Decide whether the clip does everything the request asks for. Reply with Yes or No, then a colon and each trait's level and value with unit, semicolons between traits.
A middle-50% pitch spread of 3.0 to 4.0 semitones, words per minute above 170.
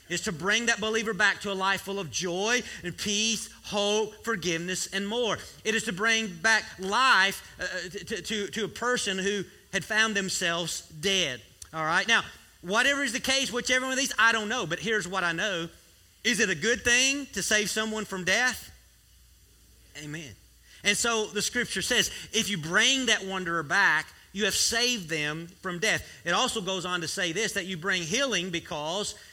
Yes: average, 3.6 semitones; average, 190 wpm